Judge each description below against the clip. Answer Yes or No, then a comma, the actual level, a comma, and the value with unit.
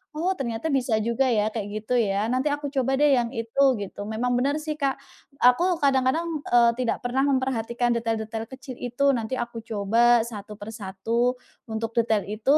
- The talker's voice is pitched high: Yes, high, 240 Hz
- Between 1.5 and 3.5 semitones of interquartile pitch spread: Yes, average, 3.1 semitones